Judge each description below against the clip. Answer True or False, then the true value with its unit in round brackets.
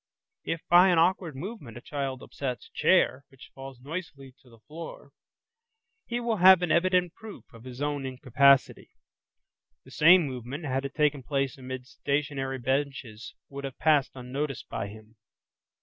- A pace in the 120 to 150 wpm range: False (160 wpm)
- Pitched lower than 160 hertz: True (140 Hz)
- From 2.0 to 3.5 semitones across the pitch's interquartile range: False (3.9 semitones)